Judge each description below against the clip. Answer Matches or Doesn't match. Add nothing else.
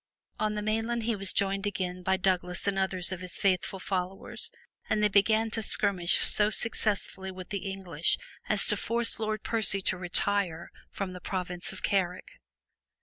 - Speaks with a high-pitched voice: Matches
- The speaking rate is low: Doesn't match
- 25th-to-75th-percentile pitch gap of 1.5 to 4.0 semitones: Matches